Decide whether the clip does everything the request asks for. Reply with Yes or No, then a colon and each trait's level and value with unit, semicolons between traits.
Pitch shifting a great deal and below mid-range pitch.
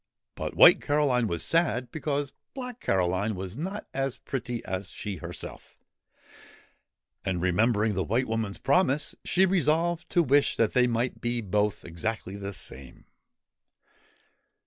Yes: wide, 6.7 semitones; low, 120 Hz